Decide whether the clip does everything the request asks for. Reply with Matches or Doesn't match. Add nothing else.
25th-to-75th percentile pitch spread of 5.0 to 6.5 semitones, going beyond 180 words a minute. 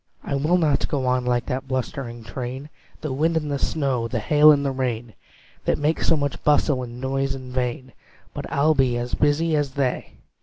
Doesn't match